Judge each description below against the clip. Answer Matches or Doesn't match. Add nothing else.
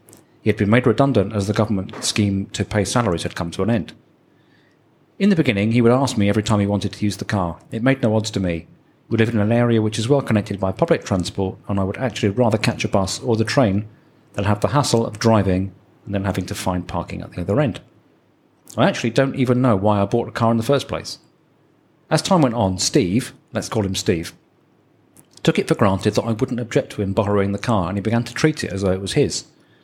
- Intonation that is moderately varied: Matches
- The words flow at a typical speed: Doesn't match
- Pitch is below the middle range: Matches